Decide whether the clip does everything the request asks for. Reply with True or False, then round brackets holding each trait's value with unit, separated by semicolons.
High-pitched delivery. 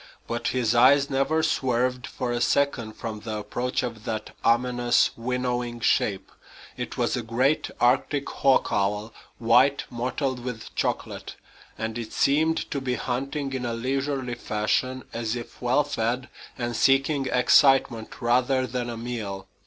False (125 Hz)